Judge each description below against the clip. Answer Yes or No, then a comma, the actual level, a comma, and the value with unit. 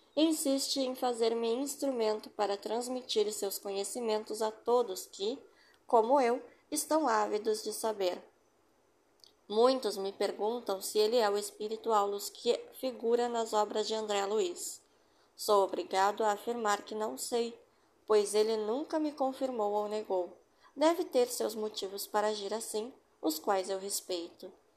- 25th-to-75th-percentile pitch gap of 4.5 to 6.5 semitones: No, average, 3.8 semitones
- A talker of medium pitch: No, high, 220 Hz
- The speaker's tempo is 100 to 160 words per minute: Yes, average, 140 wpm